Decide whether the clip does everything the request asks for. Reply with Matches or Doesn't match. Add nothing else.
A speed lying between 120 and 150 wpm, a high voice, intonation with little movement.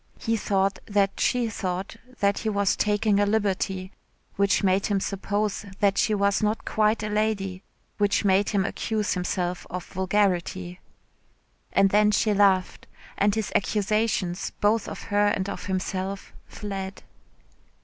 Matches